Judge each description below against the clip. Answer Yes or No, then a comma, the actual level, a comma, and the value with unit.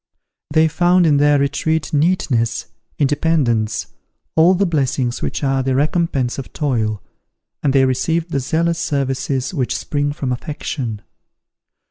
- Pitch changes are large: No, average, 3.7 semitones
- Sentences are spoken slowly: Yes, slow, 130 wpm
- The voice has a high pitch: No, medium, 140 Hz